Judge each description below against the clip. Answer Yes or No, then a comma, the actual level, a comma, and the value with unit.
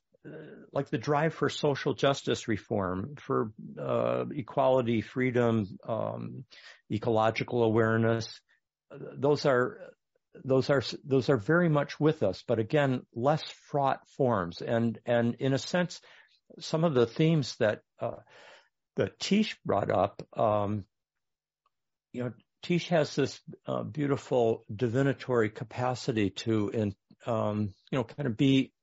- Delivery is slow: Yes, slow, 130 wpm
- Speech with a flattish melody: No, average, 4.7 semitones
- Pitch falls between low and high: No, low, 125 Hz